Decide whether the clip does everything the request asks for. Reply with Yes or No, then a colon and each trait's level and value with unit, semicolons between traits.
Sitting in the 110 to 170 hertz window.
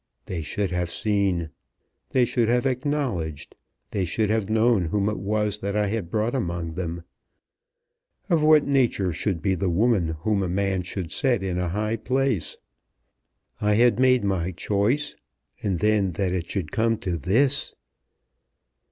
No: low, 100 Hz